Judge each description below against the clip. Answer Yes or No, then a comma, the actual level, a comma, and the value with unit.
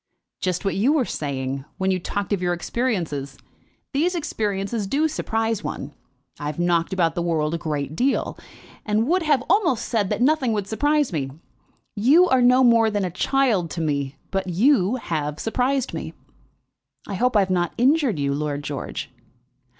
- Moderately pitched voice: No, high, 200 Hz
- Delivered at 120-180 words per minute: Yes, average, 175 wpm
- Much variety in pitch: Yes, wide, 7.3 semitones